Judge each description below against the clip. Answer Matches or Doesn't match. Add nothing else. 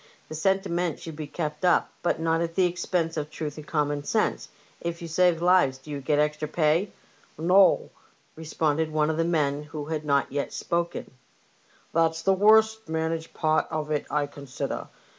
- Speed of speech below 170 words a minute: Doesn't match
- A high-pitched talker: Doesn't match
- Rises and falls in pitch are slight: Matches